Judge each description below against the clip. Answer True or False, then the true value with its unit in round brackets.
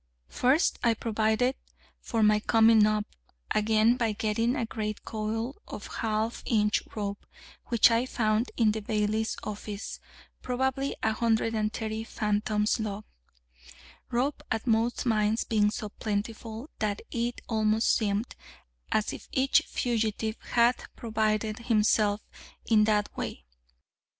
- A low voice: False (220 Hz)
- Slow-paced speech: True (120 wpm)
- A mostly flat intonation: True (1.5 semitones)